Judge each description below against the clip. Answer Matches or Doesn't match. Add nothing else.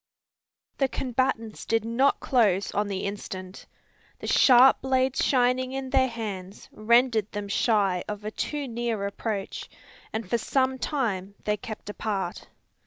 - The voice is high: Matches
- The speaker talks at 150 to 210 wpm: Doesn't match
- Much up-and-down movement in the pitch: Doesn't match